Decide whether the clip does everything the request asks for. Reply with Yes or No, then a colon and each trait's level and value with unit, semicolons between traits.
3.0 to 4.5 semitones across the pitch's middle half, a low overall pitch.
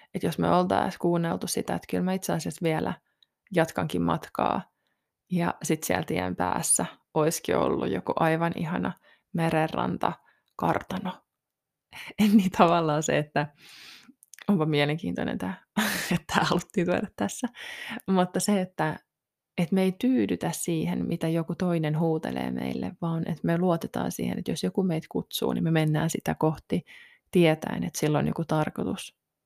No: average, 3.4 semitones; medium, 165 Hz